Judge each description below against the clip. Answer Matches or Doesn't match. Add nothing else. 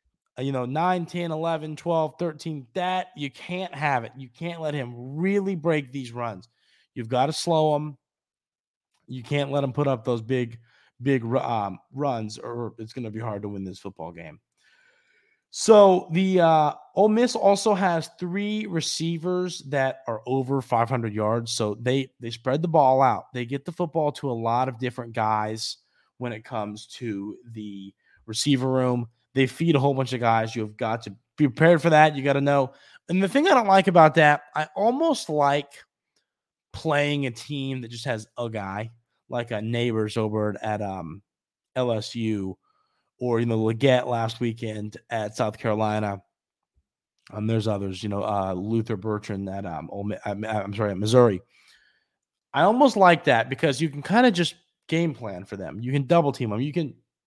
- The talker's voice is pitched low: Matches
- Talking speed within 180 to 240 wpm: Matches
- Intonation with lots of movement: Matches